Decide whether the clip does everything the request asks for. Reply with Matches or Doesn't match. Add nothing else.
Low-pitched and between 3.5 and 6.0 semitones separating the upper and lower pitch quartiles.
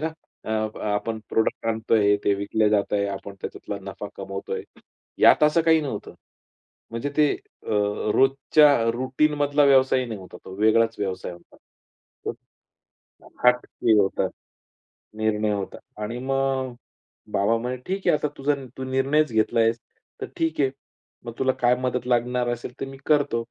Matches